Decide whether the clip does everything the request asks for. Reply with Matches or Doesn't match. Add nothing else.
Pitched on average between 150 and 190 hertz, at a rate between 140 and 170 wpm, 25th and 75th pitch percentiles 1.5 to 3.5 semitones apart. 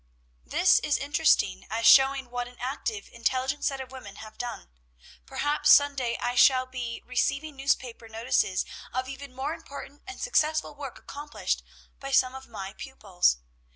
Doesn't match